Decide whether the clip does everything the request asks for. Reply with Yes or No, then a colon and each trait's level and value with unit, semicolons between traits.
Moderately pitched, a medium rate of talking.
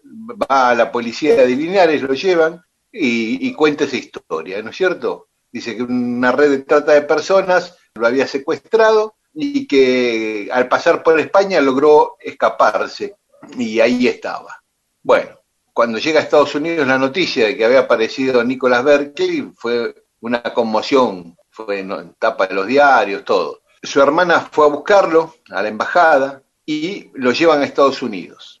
Yes: medium, 160 Hz; average, 160 wpm